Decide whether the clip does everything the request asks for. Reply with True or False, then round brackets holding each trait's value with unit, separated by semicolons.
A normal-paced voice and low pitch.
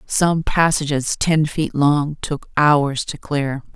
False (145 wpm; 150 Hz)